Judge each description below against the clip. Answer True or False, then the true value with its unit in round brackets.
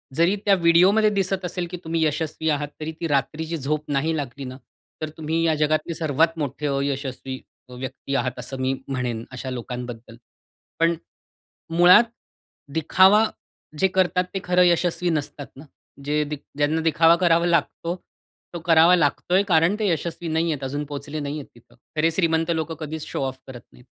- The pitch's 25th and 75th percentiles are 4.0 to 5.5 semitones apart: False (3.4 semitones)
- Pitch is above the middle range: False (160 Hz)